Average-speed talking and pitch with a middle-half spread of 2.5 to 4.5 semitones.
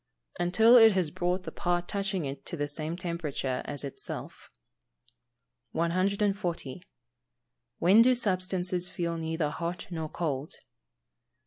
No: slow, 125 wpm; average, 2.9 semitones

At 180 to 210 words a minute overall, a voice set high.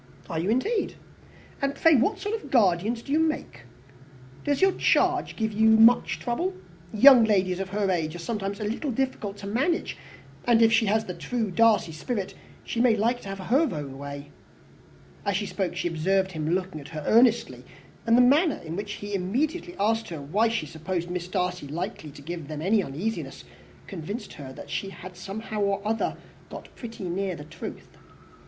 Yes: average, 190 wpm; high, 205 Hz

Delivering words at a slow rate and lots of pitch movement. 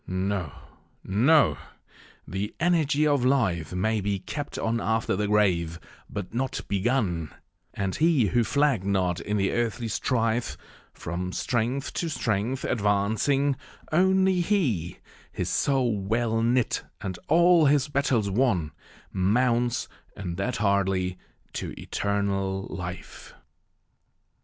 Yes: slow, 120 wpm; wide, 5.7 semitones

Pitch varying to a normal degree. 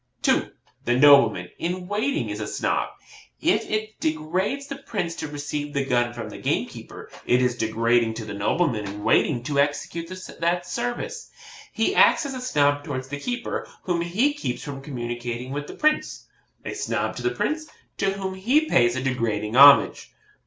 No: wide, 8.2 semitones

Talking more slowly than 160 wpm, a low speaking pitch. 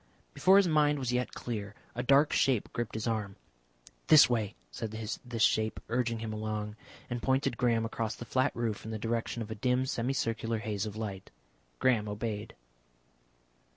No: average, 170 wpm; low, 115 Hz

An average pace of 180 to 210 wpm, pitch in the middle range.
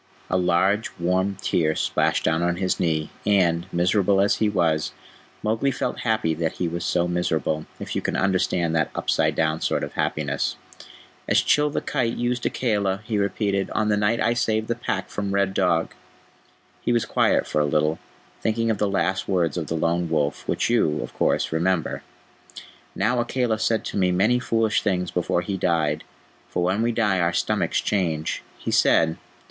No: average, 185 wpm; very low, 95 Hz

